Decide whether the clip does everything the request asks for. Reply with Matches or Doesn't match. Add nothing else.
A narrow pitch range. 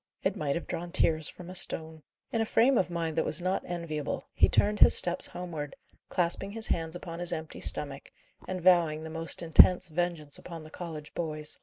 Matches